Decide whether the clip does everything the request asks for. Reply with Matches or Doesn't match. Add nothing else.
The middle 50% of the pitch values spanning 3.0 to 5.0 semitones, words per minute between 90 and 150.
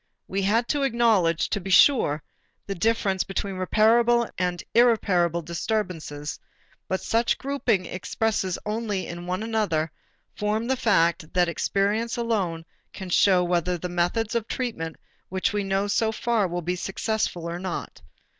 Matches